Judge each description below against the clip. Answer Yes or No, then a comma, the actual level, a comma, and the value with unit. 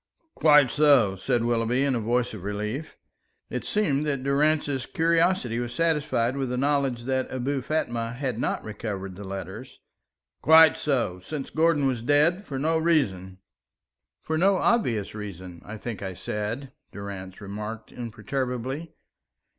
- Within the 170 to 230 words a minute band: No, average, 145 wpm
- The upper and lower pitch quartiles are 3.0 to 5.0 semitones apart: No, wide, 5.5 semitones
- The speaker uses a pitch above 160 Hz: No, low, 125 Hz